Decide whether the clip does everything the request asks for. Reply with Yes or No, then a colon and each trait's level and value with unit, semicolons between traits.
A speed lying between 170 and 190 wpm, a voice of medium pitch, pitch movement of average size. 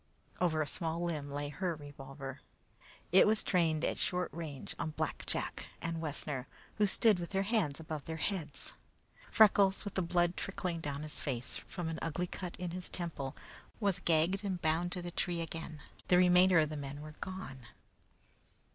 Yes: average, 180 wpm; medium, 170 Hz; average, 3.3 semitones